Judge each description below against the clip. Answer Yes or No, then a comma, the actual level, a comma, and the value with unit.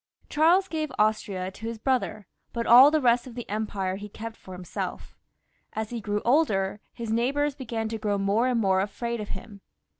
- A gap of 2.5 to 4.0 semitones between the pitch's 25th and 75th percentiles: Yes, average, 3.4 semitones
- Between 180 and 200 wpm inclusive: Yes, average, 190 wpm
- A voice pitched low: No, high, 225 Hz